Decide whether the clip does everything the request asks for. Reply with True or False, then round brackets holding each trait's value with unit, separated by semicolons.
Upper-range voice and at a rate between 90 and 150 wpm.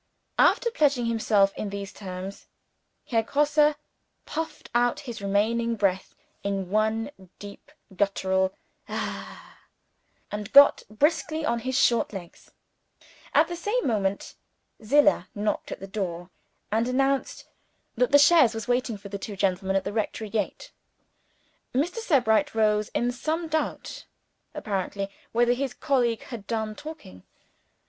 True (225 Hz; 135 wpm)